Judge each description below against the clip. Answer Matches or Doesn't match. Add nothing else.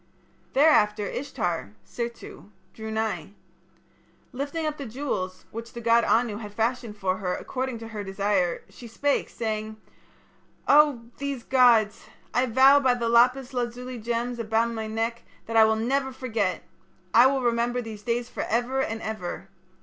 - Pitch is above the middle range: Matches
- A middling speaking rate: Matches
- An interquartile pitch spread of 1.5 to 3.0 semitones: Matches